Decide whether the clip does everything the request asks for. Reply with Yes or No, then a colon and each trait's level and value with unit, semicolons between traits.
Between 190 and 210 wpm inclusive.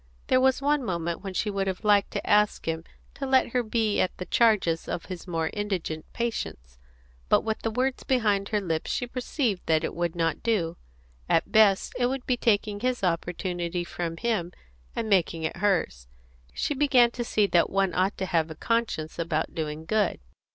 Yes: average, 195 wpm